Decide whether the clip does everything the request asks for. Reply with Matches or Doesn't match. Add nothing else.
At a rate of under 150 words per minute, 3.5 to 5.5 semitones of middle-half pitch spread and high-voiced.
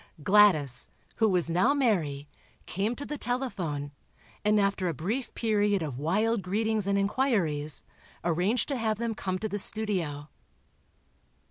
Matches